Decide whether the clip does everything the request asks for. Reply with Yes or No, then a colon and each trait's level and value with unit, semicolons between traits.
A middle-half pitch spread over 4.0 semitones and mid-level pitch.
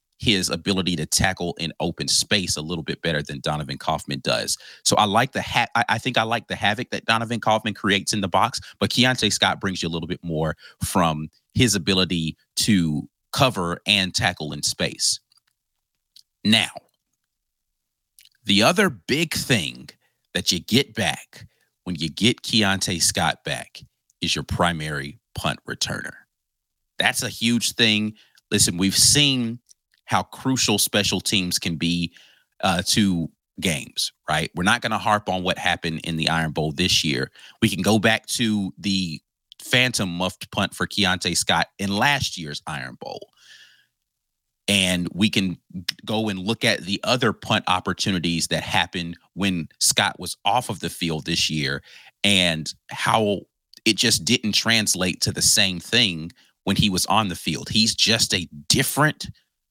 No: average, 4.4 semitones; very low, 95 Hz